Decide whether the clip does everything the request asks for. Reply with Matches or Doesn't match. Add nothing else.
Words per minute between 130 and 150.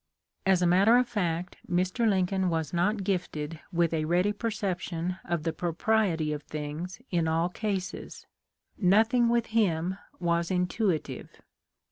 Matches